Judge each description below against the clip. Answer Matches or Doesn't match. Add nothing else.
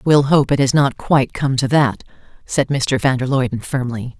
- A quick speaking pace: Matches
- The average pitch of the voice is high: Doesn't match